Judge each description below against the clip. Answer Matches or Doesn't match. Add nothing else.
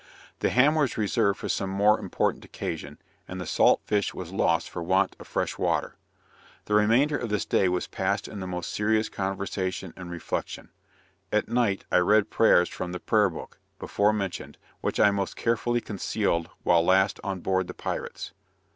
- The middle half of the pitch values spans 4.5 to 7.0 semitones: Doesn't match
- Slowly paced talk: Doesn't match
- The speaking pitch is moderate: Doesn't match